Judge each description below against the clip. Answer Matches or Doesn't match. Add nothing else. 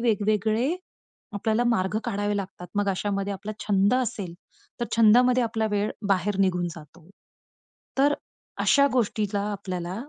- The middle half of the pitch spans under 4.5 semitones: Matches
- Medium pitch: Doesn't match